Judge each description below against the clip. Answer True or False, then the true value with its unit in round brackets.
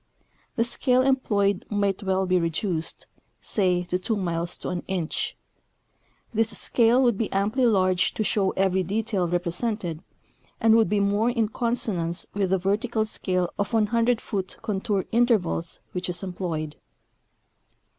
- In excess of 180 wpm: False (145 wpm)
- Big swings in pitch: False (3.7 semitones)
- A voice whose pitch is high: True (200 Hz)